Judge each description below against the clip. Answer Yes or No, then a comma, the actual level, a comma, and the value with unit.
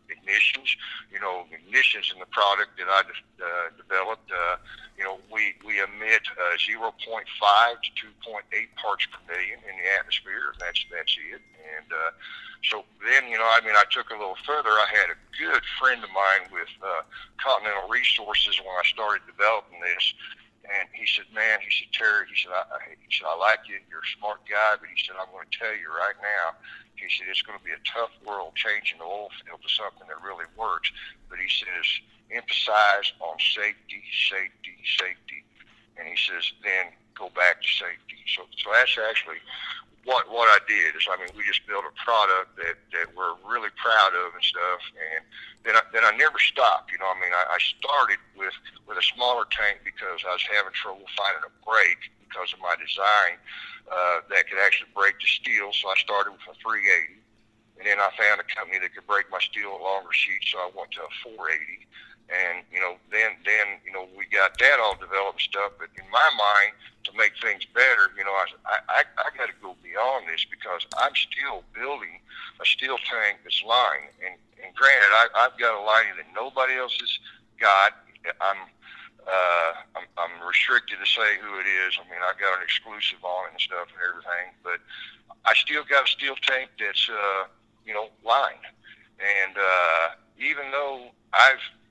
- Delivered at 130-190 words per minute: No, average, 200 wpm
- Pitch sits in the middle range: No, low, 125 Hz